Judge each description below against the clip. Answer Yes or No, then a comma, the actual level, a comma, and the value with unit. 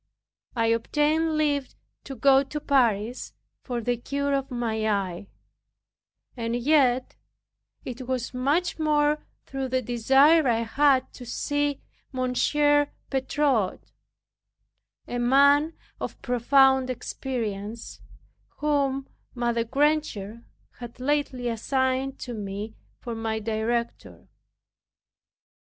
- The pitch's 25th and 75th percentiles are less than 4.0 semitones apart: Yes, average, 3.3 semitones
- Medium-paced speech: No, slow, 105 wpm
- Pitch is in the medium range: No, very high, 255 Hz